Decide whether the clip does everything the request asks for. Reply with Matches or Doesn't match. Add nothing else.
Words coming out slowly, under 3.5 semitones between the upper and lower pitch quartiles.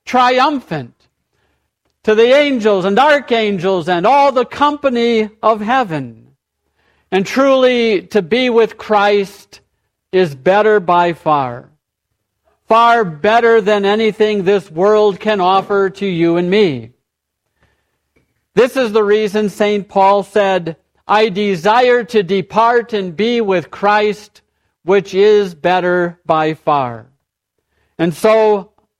Doesn't match